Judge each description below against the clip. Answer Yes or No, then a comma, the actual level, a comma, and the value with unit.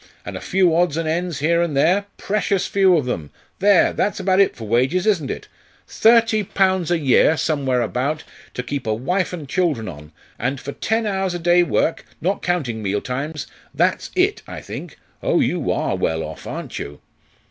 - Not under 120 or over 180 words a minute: No, average, 190 wpm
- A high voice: No, medium, 165 Hz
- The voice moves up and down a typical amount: No, wide, 6.4 semitones